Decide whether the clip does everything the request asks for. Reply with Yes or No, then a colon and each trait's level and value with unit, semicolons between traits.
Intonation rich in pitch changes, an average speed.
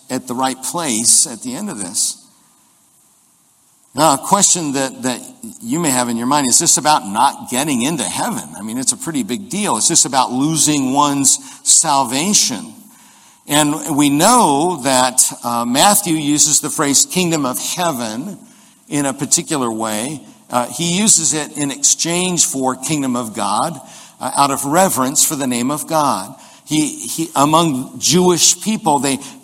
Yes: wide, 7.7 semitones; average, 165 wpm